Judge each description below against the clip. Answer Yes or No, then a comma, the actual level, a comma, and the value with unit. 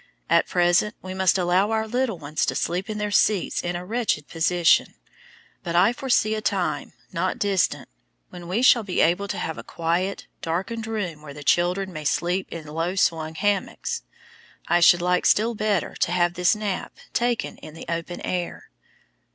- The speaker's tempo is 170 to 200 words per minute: Yes, average, 180 wpm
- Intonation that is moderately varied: Yes, average, 3.6 semitones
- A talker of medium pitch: Yes, medium, 180 Hz